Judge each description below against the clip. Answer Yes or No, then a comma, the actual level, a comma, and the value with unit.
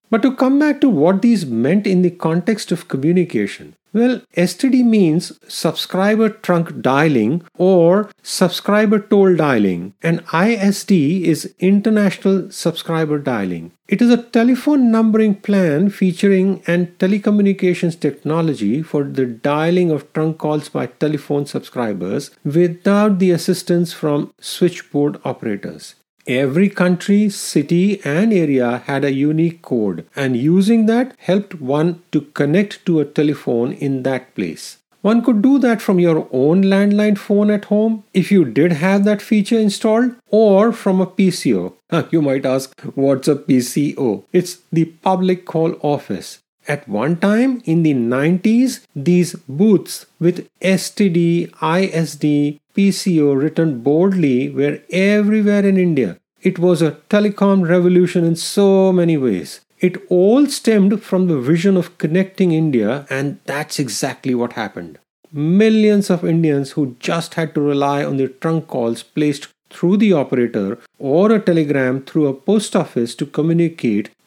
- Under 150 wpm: Yes, average, 140 wpm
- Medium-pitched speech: Yes, medium, 175 Hz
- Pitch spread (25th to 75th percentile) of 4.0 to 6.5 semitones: Yes, average, 5.1 semitones